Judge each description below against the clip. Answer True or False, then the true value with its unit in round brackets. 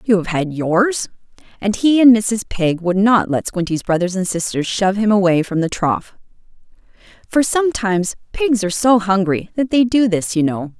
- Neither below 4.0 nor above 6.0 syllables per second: True (5.0 syllables/s)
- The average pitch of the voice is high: True (200 Hz)